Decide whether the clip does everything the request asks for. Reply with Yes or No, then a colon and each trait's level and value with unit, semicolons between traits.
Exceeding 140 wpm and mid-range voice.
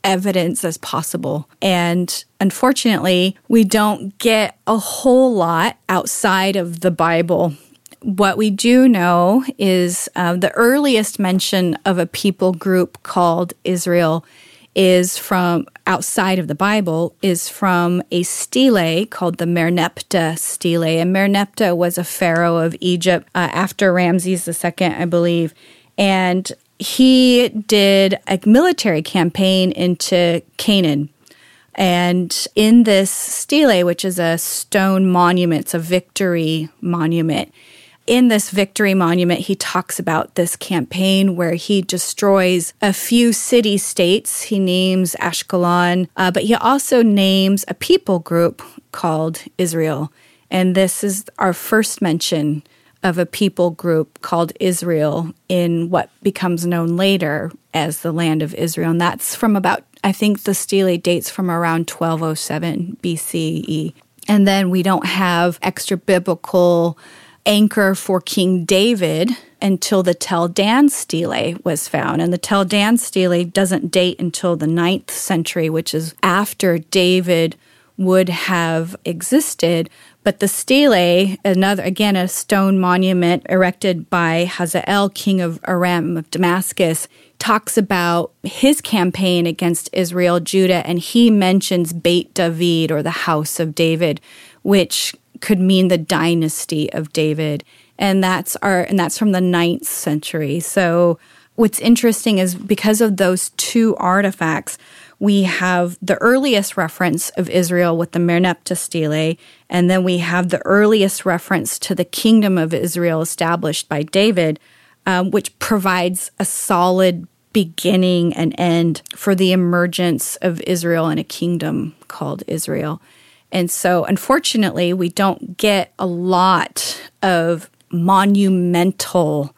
No: slow, 135 wpm; medium, 180 Hz